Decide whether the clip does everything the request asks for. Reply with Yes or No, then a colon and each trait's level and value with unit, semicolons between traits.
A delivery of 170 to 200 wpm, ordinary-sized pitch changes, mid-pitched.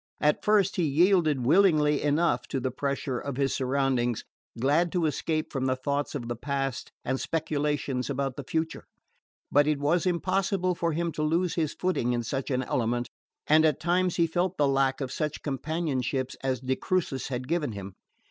Yes: average, 180 wpm; average, 4.0 semitones; medium, 145 Hz